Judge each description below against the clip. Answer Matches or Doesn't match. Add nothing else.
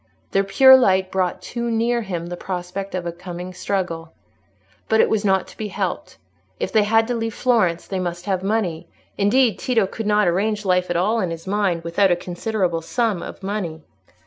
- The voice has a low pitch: Doesn't match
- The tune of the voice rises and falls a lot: Doesn't match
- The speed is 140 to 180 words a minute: Doesn't match